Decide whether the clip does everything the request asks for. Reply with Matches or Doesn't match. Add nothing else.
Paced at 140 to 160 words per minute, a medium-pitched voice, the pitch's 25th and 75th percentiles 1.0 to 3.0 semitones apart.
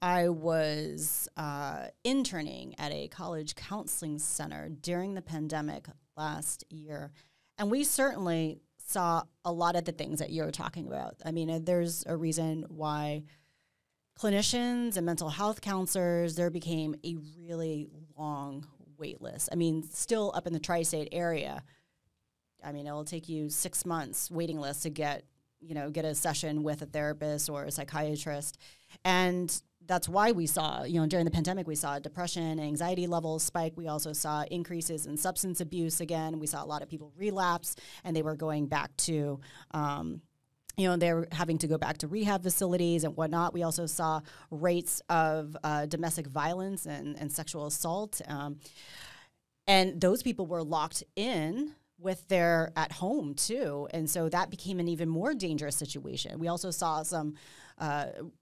Doesn't match